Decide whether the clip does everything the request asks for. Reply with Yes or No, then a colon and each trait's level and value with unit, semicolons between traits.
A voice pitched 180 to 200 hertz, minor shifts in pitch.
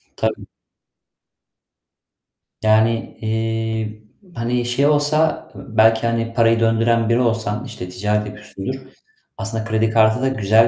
No: low, 115 Hz; narrow, 1.2 semitones